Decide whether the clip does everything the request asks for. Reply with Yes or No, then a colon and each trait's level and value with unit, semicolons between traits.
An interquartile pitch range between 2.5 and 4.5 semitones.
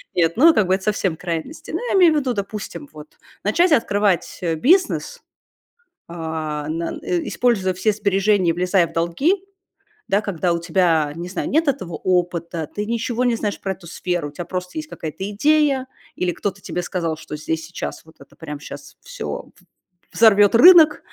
No: wide, 5.5 semitones